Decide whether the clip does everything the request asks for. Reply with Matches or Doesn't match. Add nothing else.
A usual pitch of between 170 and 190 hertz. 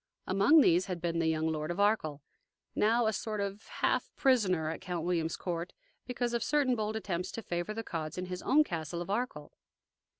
Matches